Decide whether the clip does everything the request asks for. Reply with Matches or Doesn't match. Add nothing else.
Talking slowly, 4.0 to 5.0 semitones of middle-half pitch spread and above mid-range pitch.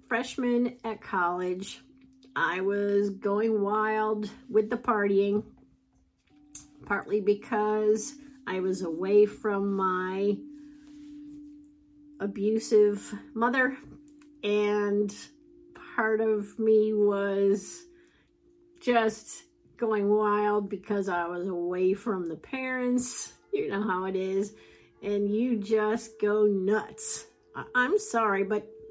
Matches